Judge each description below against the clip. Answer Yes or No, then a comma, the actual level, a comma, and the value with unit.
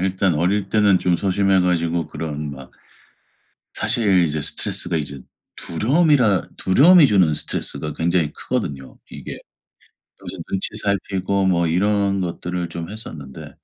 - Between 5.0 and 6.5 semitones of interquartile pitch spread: No, average, 3.5 semitones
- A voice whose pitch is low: Yes, very low, 90 Hz